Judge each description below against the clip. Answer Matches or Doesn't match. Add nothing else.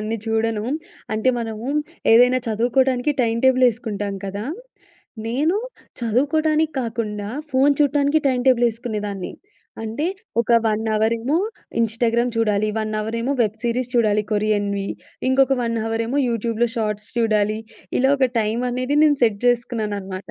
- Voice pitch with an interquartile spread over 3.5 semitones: Doesn't match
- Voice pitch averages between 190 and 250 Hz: Matches